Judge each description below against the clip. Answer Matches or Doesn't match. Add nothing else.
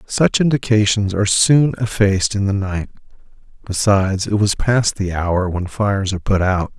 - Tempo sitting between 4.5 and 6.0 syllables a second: Matches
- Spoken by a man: Matches